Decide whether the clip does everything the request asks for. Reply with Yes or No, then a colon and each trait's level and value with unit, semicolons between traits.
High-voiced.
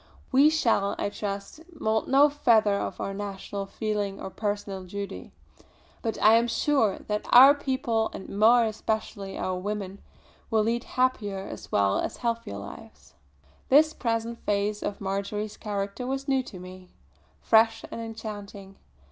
Yes: high, 215 Hz